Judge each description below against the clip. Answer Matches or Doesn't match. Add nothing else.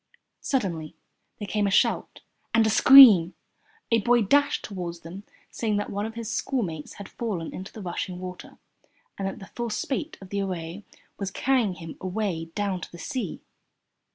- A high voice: Matches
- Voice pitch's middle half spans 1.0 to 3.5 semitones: Doesn't match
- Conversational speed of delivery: Matches